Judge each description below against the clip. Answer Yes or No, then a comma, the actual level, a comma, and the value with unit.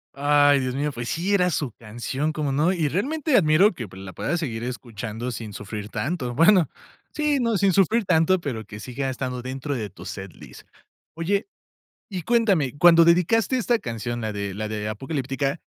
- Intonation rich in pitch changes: Yes, wide, 7.4 semitones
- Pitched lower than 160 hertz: Yes, medium, 140 Hz